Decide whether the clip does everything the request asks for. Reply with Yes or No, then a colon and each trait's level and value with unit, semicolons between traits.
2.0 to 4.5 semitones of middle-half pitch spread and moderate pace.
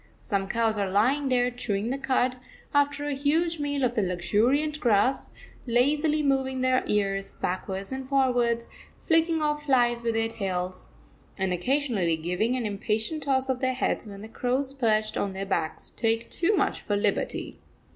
No: average, 5.1 semitones; average, 170 wpm